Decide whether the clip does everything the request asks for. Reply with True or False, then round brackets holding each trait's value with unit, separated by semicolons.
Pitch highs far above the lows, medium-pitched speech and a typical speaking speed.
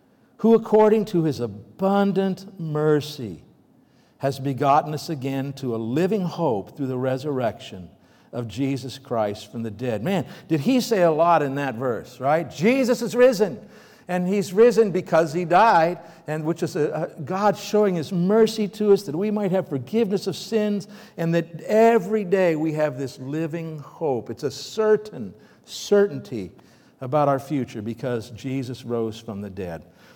True (7.0 semitones; 165 Hz; 165 wpm)